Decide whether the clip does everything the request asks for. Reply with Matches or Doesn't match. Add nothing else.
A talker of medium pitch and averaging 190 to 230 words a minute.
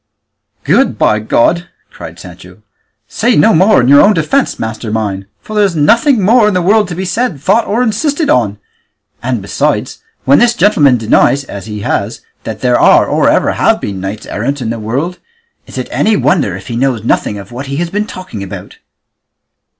Matches